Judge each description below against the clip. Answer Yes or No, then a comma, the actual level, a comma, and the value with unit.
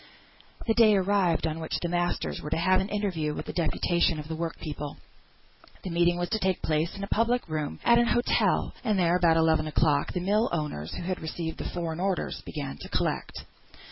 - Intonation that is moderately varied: Yes, average, 3.3 semitones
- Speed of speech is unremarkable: No, fast, 210 wpm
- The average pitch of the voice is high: No, medium, 175 Hz